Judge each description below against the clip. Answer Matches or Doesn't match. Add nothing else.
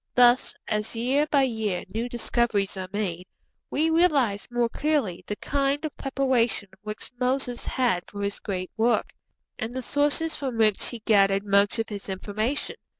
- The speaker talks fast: Doesn't match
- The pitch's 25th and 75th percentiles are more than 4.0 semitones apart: Matches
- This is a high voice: Matches